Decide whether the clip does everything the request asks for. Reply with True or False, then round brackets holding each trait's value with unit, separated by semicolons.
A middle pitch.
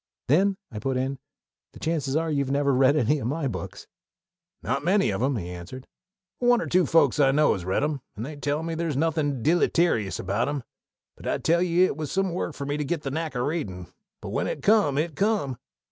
True (145 Hz)